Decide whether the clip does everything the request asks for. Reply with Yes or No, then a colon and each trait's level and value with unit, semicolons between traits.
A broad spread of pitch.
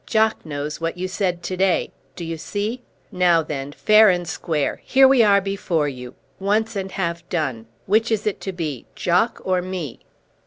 No: average, 4.1 semitones